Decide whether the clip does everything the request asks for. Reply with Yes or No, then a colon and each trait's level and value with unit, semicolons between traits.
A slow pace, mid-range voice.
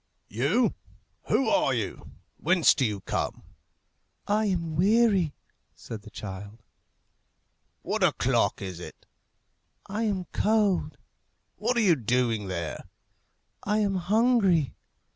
Yes: slow, 115 wpm; medium, 175 Hz